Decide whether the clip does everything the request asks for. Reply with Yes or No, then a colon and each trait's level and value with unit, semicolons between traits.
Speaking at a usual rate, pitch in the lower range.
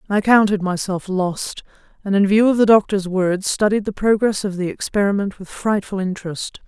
No: average, 180 wpm; high, 200 Hz